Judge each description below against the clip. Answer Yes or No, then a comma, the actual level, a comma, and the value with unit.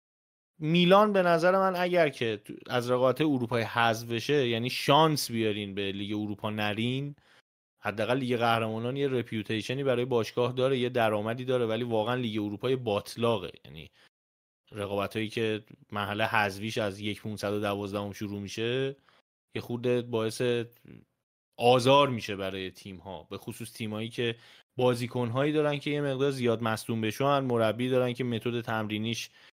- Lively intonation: No, average, 3.0 semitones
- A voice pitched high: No, low, 115 Hz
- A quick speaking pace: No, average, 145 wpm